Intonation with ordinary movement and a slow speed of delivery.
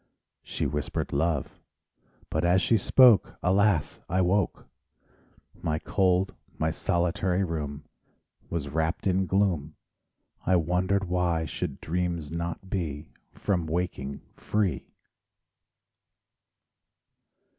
Yes: average, 3.0 semitones; slow, 100 wpm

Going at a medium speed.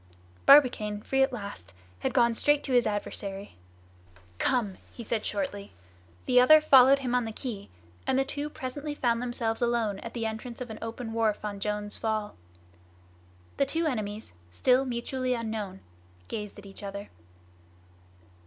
Yes: average, 155 wpm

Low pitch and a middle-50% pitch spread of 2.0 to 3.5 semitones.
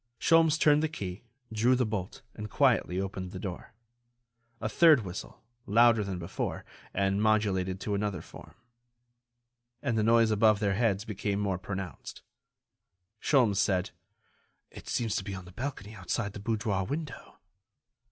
Yes: low, 105 Hz; average, 3.1 semitones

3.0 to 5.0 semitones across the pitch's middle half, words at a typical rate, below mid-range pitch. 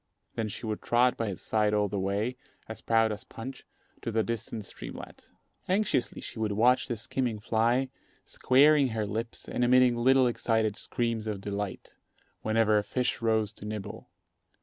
No: narrow, 2.5 semitones; average, 170 wpm; low, 115 Hz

